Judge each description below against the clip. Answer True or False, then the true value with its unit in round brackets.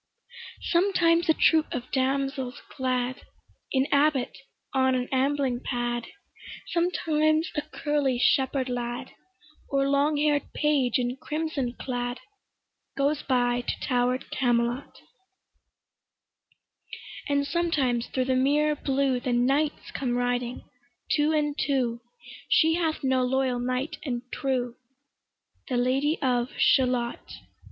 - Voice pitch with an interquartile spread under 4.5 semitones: True (3.0 semitones)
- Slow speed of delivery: True (115 wpm)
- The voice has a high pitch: True (265 Hz)